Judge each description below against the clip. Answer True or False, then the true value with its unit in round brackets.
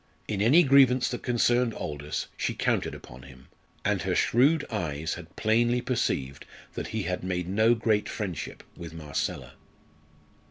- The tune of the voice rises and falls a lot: True (7.0 semitones)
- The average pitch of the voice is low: True (105 Hz)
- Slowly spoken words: False (150 wpm)